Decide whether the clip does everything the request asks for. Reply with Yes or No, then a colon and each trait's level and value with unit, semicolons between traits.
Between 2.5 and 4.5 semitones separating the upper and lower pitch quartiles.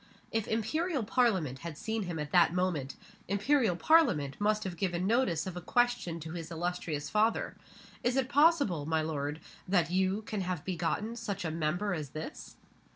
No: wide, 5.4 semitones